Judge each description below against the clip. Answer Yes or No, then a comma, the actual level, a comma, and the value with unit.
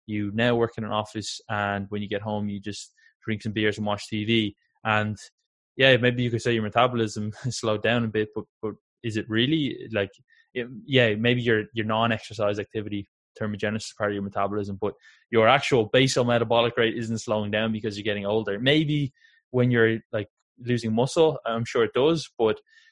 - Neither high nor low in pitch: No, low, 110 Hz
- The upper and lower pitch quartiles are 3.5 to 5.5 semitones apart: No, narrow, 2.5 semitones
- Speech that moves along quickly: No, average, 195 wpm